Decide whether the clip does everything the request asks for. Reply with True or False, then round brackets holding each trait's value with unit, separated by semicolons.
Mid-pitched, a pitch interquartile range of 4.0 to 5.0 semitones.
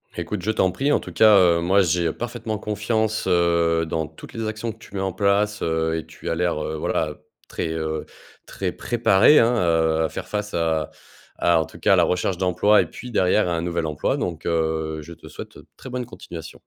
False (90 Hz; 4.6 semitones)